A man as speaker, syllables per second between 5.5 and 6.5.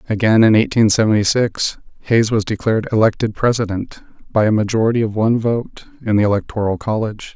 Yes: male; 6.0 syllables/s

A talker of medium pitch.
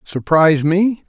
Yes: medium, 170 Hz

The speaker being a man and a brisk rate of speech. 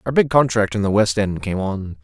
Yes: male; fast, 265 wpm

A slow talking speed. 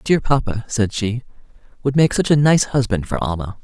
No: average, 200 wpm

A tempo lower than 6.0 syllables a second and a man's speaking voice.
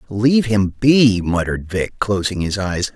Yes: 4.6 syllables/s; male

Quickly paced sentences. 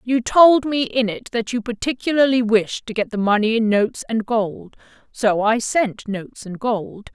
No: average, 195 wpm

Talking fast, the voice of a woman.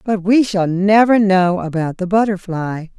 No: average, 160 wpm; female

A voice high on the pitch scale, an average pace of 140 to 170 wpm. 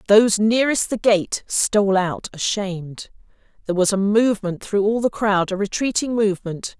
Yes: high, 205 Hz; average, 150 wpm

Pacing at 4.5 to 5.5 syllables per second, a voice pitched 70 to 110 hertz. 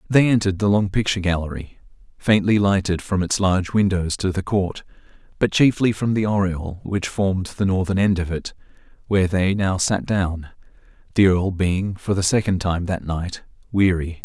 Yes: 5.0 syllables/s; very low, 95 Hz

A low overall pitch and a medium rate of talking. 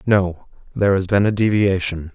Yes: very low, 95 Hz; average, 170 wpm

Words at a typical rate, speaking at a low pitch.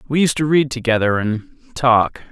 Yes: average, 180 wpm; low, 125 Hz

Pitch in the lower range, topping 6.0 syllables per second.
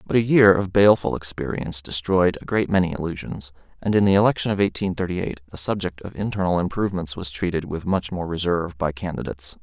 Yes: very low, 90 Hz; 6.3 syllables/s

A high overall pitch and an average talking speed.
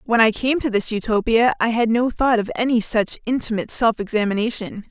Yes: high, 225 Hz; average, 195 wpm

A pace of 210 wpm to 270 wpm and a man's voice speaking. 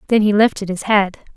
No: fast, 220 wpm; female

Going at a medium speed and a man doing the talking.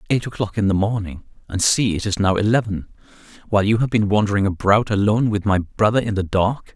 No: fast, 215 wpm; male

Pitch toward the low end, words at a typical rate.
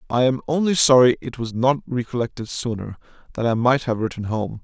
Yes: low, 125 Hz; average, 195 wpm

